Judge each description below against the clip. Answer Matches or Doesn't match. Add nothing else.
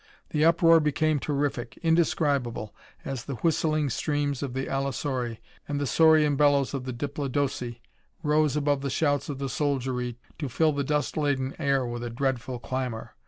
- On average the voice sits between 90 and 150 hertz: Matches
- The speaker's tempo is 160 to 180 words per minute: Matches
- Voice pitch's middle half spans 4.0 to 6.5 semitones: Doesn't match